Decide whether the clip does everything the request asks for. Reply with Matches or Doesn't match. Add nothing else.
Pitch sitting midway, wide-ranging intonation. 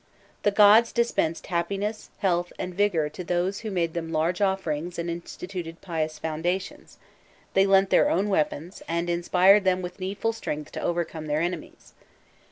Doesn't match